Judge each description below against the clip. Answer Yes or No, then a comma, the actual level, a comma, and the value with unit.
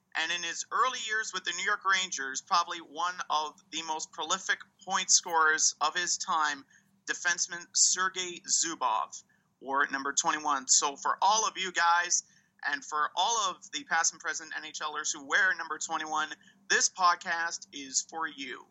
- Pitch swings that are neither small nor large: Yes, average, 3.4 semitones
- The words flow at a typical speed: Yes, average, 170 wpm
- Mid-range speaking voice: Yes, medium, 170 Hz